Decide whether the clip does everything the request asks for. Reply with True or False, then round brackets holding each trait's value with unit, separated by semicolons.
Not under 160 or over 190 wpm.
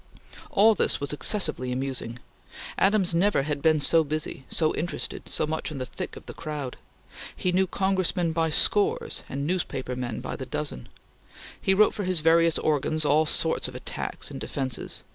True (175 wpm)